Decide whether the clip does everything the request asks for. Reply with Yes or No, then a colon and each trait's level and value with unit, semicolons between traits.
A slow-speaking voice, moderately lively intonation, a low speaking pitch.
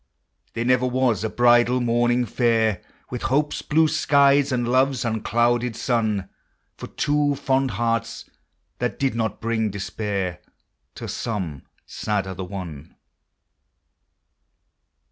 Yes: slow, 115 wpm; average, 3.3 semitones; low, 120 Hz